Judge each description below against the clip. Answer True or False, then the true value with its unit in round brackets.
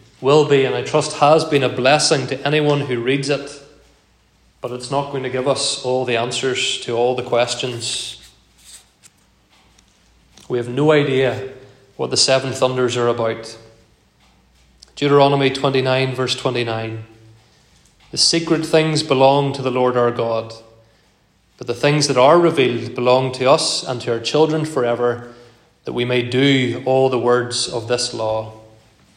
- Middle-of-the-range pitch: False (125 Hz)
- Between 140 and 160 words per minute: True (155 wpm)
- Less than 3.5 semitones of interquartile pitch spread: True (2.8 semitones)